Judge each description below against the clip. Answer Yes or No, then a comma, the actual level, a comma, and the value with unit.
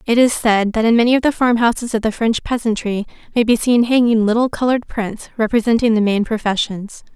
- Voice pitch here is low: No, high, 225 Hz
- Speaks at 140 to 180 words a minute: No, average, 200 wpm